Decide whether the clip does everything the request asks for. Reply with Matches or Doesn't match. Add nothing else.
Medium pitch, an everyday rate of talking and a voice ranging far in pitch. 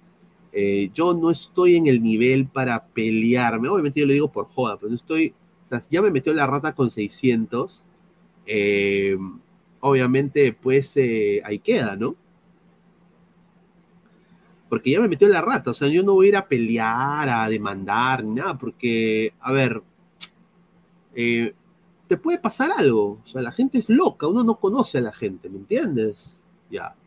Matches